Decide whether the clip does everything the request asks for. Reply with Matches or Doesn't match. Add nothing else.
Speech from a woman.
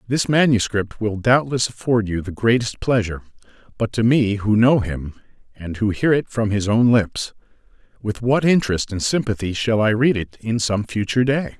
Doesn't match